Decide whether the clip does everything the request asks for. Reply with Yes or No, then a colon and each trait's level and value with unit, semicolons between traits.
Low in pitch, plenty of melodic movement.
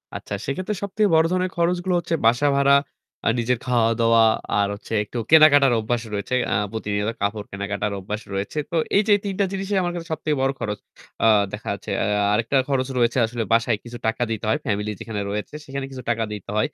Yes: low, 120 Hz; wide, 6.5 semitones